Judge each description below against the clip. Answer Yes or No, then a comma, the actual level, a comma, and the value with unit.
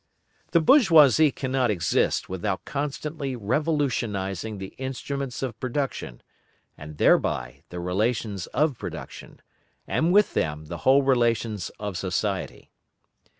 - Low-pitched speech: Yes, low, 120 Hz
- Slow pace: Yes, slow, 110 wpm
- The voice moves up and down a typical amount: No, wide, 6.6 semitones